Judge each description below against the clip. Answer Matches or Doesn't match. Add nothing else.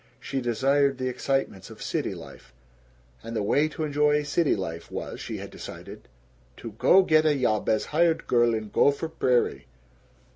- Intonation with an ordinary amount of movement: Matches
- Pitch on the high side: Doesn't match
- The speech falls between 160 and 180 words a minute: Matches